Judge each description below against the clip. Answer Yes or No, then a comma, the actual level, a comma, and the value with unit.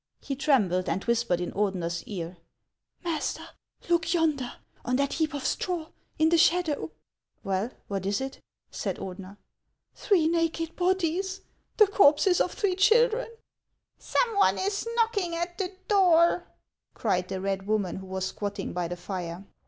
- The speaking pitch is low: No, very high, 290 Hz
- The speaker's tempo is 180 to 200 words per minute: No, average, 170 wpm